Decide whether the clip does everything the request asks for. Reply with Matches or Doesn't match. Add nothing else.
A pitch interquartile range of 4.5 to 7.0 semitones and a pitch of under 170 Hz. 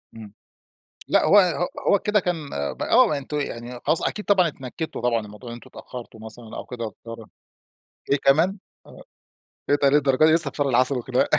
Matches